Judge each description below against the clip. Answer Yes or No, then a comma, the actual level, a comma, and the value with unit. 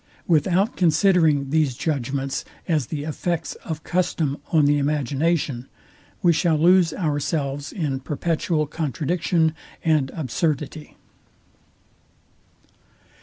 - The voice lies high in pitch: No, medium, 155 Hz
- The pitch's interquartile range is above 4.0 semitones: No, average, 2.9 semitones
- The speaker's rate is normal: No, slow, 95 wpm